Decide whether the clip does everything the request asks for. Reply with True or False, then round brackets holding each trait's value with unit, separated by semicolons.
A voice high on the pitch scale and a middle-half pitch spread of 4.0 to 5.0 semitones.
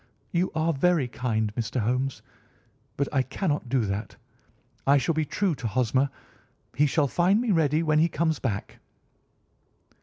False (140 Hz; 4.7 semitones)